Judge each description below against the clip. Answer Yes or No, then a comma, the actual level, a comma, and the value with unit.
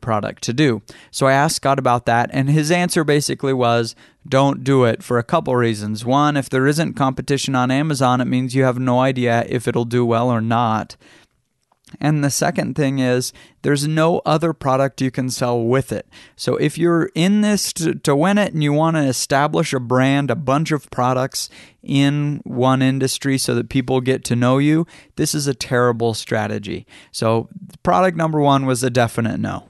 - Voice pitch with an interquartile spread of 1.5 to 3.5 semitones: Yes, average, 3.2 semitones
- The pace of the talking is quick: No, average, 195 wpm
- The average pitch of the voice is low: Yes, low, 130 Hz